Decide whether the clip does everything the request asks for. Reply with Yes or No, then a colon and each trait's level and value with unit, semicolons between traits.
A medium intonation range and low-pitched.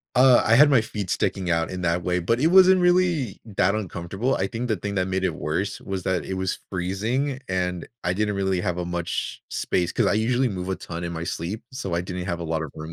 Yes: average, 4.5 semitones; very low, 95 Hz